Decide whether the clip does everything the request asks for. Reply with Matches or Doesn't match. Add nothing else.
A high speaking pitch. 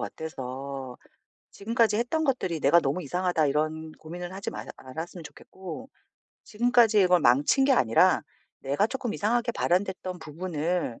Doesn't match